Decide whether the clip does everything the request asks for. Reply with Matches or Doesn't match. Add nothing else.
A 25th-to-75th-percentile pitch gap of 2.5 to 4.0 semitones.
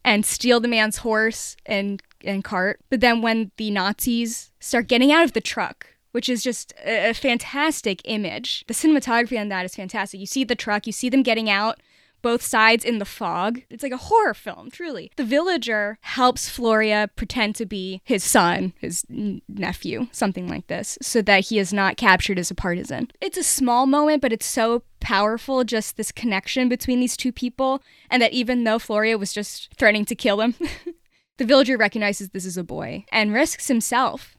Matches